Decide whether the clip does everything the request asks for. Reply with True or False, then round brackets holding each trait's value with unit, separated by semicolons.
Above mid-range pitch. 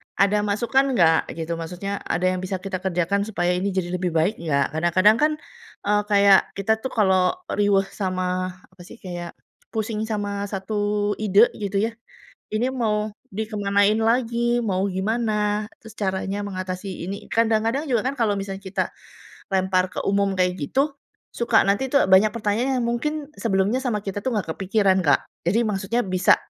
True (200 Hz)